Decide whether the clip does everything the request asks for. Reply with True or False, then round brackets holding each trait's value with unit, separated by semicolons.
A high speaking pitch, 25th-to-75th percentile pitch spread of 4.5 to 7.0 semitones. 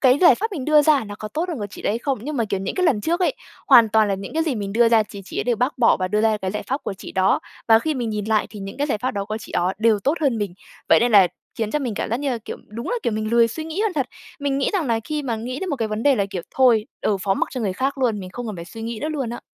True (230 Hz; 4.9 semitones)